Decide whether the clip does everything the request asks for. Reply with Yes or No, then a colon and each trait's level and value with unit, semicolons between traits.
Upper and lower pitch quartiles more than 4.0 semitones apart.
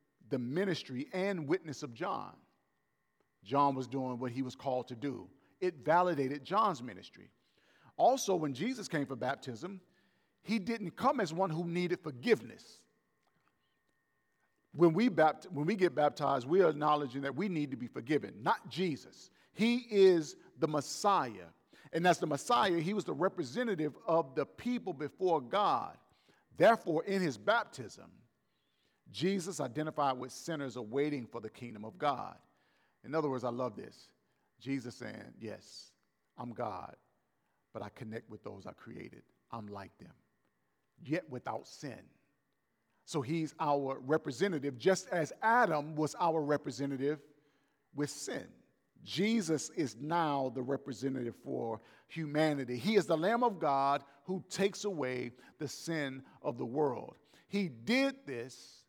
Yes: average, 5.2 semitones